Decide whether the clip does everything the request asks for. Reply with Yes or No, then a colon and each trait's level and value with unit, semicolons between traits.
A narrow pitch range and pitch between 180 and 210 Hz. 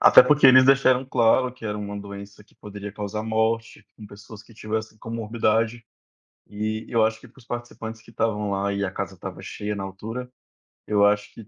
No: narrow, 1.9 semitones; low, 110 Hz